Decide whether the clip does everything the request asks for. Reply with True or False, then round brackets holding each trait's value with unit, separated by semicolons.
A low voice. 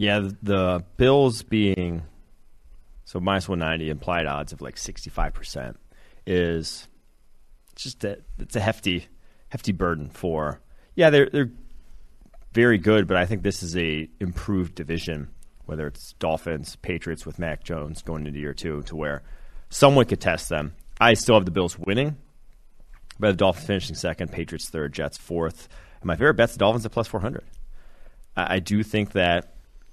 True (90 Hz)